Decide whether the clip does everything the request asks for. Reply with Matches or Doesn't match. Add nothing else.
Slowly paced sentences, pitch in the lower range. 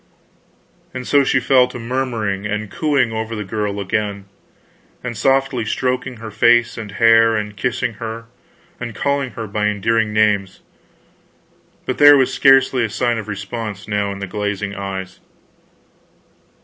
Doesn't match